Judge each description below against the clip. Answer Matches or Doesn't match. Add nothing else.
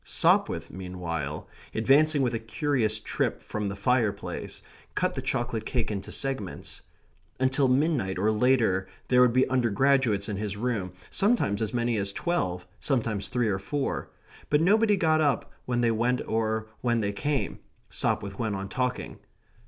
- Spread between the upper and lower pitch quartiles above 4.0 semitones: Matches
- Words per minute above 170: Doesn't match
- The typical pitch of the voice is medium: Doesn't match